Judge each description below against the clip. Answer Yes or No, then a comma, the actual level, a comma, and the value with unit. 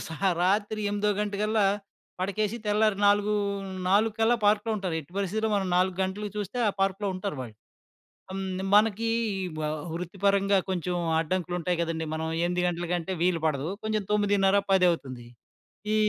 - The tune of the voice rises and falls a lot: No, average, 2.8 semitones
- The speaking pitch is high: Yes, high, 195 Hz